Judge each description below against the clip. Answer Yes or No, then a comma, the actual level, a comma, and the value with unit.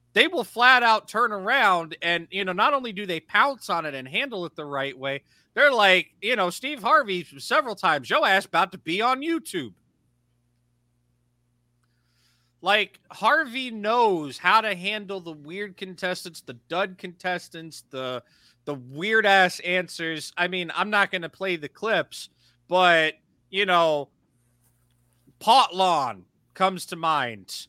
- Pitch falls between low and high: Yes, medium, 175 Hz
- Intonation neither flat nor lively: No, wide, 6.8 semitones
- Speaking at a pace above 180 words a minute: No, average, 155 wpm